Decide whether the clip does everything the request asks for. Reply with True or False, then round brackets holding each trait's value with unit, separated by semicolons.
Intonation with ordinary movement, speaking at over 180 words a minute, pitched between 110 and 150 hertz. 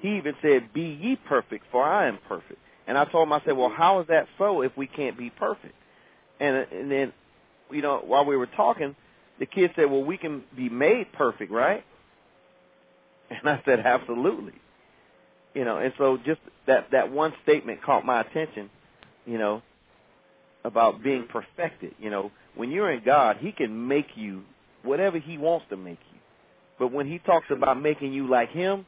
True (4.4 semitones; 190 wpm; 140 Hz)